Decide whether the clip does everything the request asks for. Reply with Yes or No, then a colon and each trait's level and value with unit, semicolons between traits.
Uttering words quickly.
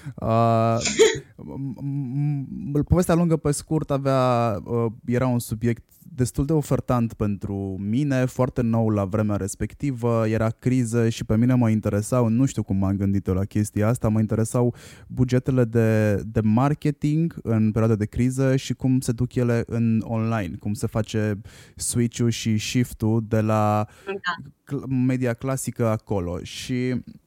No: average, 145 wpm